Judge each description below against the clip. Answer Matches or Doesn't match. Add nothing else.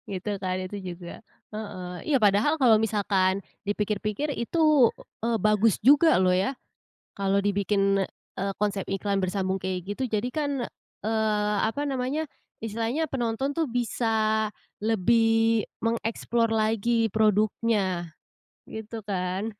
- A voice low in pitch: Doesn't match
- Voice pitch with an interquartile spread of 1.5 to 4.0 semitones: Matches